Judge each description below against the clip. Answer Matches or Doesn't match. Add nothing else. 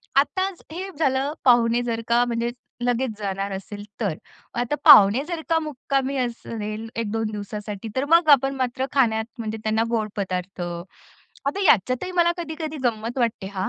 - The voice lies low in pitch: Doesn't match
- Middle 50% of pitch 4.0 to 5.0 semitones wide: Matches